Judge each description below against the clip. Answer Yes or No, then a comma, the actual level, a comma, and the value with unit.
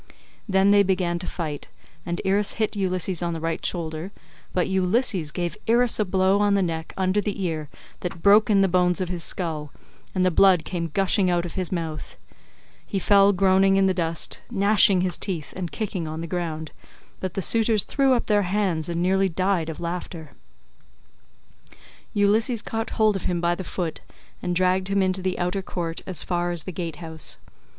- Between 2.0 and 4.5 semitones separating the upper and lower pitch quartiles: Yes, narrow, 2.5 semitones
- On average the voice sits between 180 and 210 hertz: Yes, medium, 185 Hz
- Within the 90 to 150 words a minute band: No, average, 195 wpm